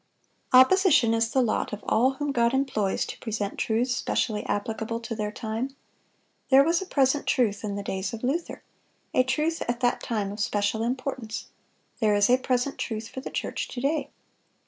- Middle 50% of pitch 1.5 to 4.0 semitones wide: Yes, average, 3.6 semitones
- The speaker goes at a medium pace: Yes, average, 180 wpm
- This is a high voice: Yes, high, 240 Hz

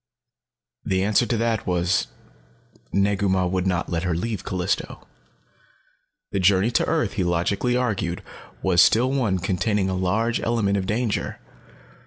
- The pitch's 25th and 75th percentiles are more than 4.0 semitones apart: No, average, 3.5 semitones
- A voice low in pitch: Yes, low, 100 Hz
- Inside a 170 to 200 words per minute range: No, average, 145 wpm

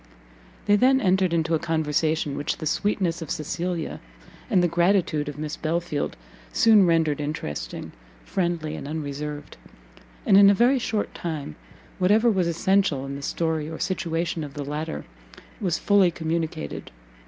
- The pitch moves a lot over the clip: No, average, 3.6 semitones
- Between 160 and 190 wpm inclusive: No, average, 150 wpm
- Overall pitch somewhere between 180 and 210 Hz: No, medium, 165 Hz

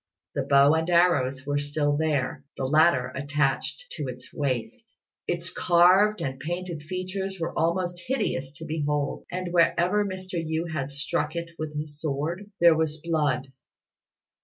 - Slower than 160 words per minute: Yes, average, 150 wpm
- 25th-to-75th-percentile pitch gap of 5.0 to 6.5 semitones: No, average, 3.5 semitones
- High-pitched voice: No, medium, 160 Hz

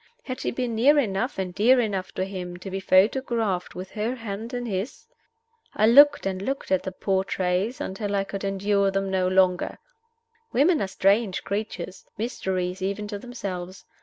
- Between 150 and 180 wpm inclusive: Yes, average, 170 wpm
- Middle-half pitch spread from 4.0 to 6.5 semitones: No, average, 3.5 semitones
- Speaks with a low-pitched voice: No, high, 195 Hz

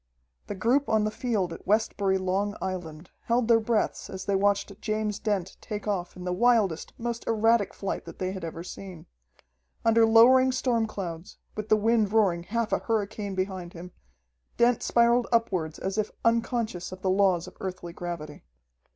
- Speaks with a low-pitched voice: No, high, 205 Hz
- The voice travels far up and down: No, average, 3.5 semitones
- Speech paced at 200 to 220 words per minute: No, average, 175 wpm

